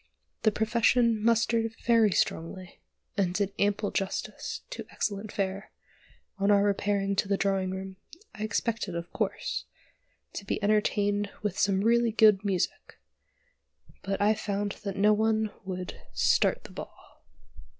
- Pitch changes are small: Yes, narrow, 1.8 semitones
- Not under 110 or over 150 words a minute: Yes, average, 140 wpm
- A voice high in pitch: Yes, high, 205 Hz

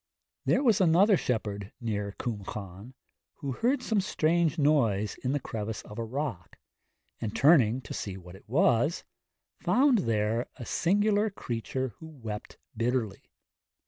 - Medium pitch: No, low, 125 Hz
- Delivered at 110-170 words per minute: Yes, average, 145 wpm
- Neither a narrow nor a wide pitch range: No, wide, 7.6 semitones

